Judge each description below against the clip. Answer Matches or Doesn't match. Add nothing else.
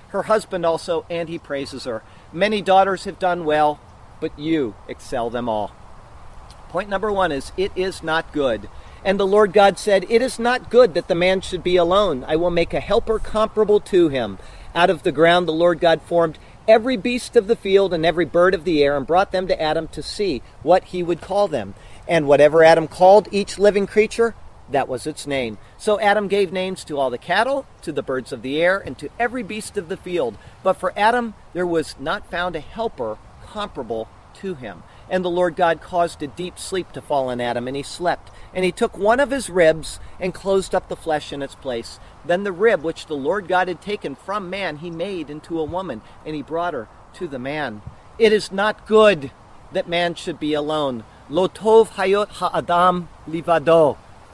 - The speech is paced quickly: Matches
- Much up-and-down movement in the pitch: Doesn't match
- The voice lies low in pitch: Doesn't match